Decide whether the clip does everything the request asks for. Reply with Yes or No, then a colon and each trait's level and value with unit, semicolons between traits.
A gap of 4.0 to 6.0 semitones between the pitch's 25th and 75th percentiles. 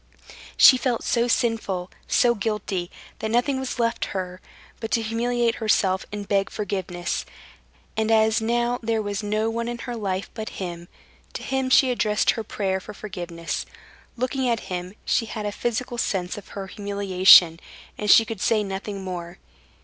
No: average, 3.5 semitones